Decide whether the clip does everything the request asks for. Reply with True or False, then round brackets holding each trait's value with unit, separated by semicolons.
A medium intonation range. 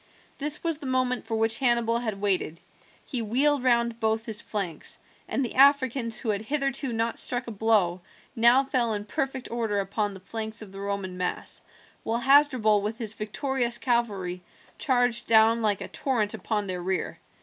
True (3.3 semitones)